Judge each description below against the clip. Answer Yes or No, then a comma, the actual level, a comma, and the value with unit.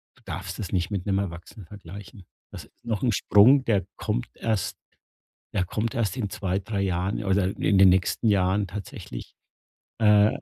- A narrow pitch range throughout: Yes, narrow, 2.3 semitones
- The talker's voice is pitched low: Yes, low, 100 Hz